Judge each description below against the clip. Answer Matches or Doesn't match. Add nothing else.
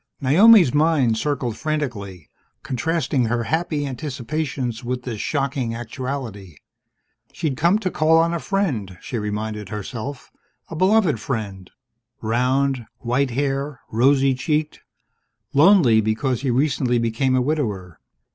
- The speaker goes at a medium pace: Doesn't match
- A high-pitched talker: Doesn't match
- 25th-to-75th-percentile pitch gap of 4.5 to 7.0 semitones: Matches